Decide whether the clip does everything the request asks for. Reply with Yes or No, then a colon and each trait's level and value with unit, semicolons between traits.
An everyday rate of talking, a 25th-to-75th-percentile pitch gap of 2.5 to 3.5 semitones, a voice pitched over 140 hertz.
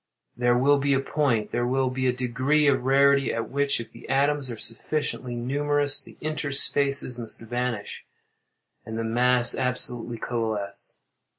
No: average, 150 wpm; average, 2.8 semitones; low, 130 Hz